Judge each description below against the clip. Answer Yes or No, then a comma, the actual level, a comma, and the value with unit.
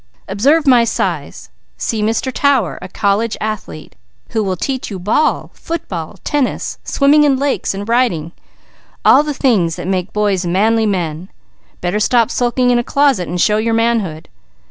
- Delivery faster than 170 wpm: No, average, 160 wpm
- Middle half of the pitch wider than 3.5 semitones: Yes, average, 5.3 semitones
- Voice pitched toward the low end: No, high, 220 Hz